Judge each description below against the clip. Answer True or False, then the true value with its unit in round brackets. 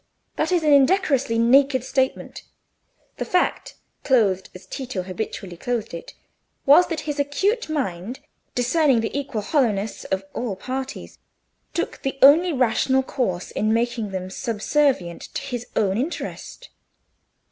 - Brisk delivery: False (135 wpm)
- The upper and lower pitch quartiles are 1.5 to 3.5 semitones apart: False (5.1 semitones)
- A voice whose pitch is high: True (255 Hz)